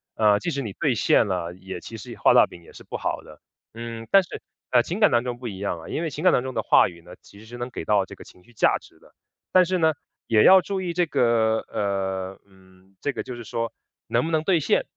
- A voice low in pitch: Yes, low, 115 Hz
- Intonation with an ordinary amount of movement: No, wide, 7.8 semitones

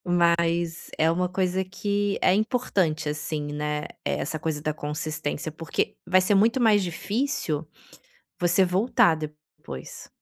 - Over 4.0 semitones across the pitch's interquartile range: No, average, 3.7 semitones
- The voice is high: No, medium, 170 Hz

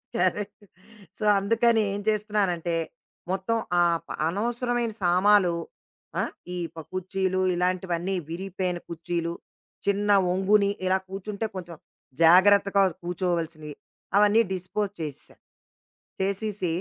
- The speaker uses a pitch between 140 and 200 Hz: Yes, high, 190 Hz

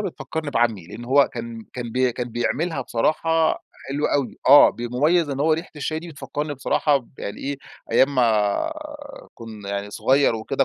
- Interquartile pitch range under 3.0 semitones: No, average, 4.1 semitones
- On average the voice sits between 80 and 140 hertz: Yes, low, 135 Hz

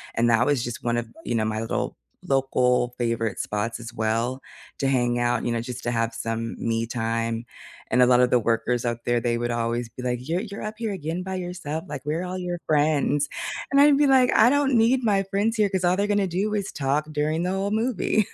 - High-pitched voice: No, low, 135 Hz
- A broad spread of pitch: Yes, wide, 8.1 semitones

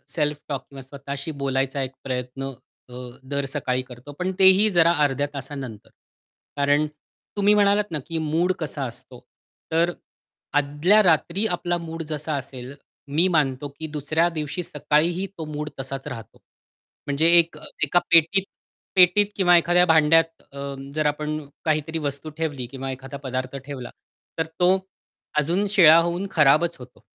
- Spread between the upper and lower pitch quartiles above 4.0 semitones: No, average, 3.7 semitones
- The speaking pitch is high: No, medium, 150 Hz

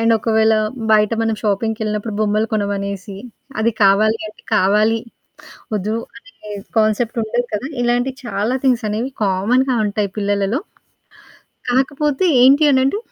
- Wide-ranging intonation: No, average, 2.9 semitones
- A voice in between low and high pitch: No, high, 220 Hz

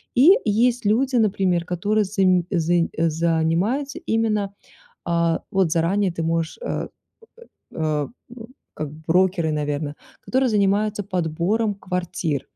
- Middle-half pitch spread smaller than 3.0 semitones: No, average, 4.4 semitones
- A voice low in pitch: No, medium, 185 Hz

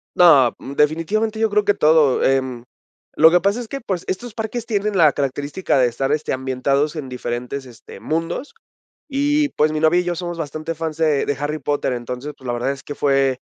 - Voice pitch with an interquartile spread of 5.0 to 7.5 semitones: Yes, wide, 5.6 semitones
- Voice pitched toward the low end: No, medium, 155 Hz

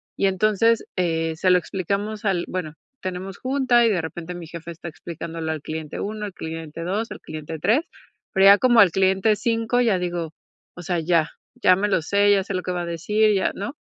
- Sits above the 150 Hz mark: Yes, medium, 185 Hz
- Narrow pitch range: No, average, 3.9 semitones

